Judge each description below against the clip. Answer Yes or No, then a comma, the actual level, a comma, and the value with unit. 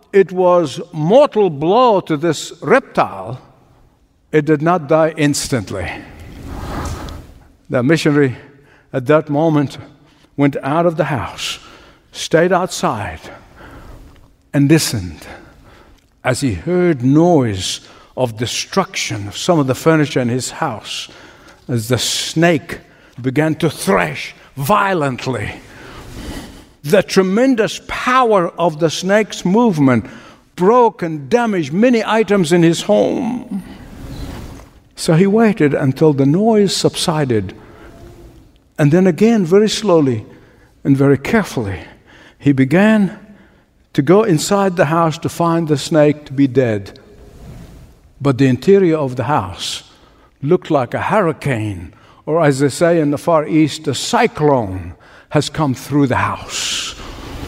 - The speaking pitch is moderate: Yes, medium, 150 Hz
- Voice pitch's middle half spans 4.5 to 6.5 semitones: Yes, average, 5.1 semitones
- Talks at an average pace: No, slow, 120 wpm